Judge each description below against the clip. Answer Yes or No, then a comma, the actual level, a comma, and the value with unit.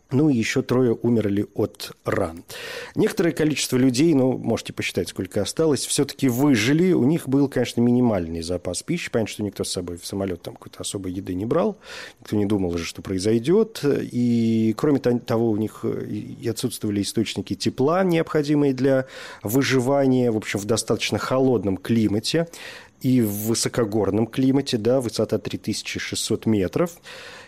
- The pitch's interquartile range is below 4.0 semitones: No, average, 4.6 semitones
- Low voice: Yes, low, 115 Hz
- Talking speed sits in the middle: Yes, average, 150 wpm